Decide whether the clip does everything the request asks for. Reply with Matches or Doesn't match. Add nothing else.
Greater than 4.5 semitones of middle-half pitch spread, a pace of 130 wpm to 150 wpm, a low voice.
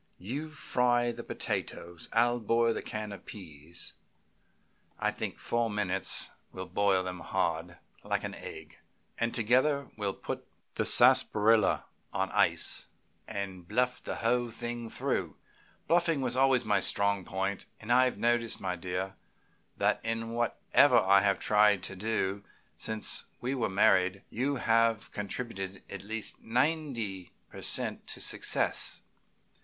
Doesn't match